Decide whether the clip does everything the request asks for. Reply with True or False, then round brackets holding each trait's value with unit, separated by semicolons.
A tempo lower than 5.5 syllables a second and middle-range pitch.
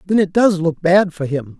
True (4.7 syllables/s; 170 Hz)